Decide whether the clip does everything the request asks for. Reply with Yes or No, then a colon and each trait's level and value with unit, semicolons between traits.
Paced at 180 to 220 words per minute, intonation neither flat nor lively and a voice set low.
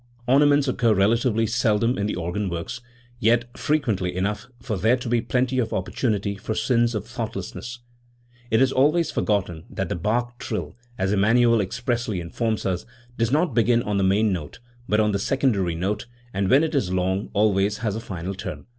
Yes: average, 185 wpm; average, 3.8 semitones; low, 110 Hz